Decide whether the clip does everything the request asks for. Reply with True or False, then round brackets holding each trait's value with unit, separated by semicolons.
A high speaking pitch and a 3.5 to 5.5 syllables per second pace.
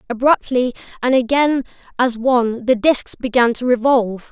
True (245 Hz; 4.9 syllables/s)